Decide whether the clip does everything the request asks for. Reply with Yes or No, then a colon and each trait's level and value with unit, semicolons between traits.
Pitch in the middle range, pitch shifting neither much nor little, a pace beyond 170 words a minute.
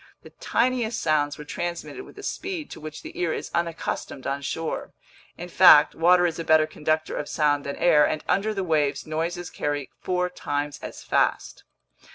Yes: medium, 160 Hz; average, 3.1 semitones; average, 185 wpm